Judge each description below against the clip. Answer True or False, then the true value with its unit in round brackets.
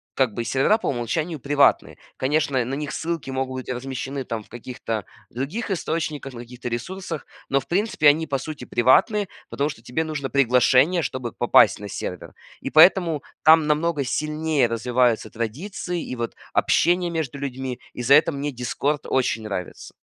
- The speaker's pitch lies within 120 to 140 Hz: True (135 Hz)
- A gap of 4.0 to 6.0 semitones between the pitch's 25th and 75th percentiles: True (4.3 semitones)